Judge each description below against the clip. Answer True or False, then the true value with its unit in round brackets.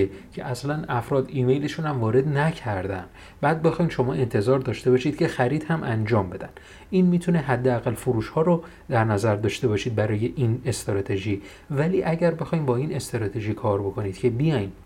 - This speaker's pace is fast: True (165 wpm)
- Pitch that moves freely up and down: True (6.2 semitones)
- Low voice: True (125 Hz)